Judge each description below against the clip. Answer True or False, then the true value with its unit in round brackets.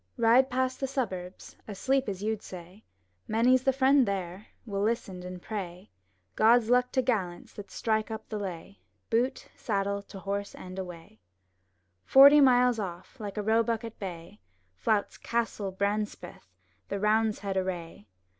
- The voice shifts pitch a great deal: False (3.8 semitones)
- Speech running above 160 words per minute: False (150 wpm)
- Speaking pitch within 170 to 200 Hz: False (210 Hz)